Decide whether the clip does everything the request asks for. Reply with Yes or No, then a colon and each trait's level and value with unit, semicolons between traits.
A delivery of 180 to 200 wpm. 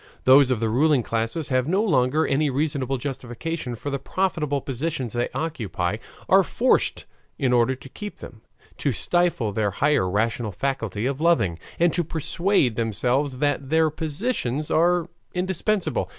No: average, 150 wpm